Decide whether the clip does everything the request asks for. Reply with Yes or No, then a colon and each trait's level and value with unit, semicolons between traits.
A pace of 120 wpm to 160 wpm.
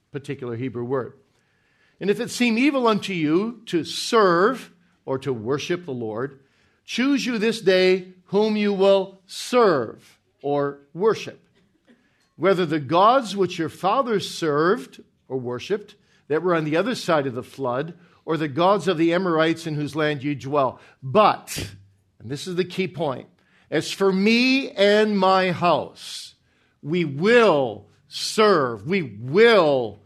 Yes: average, 150 wpm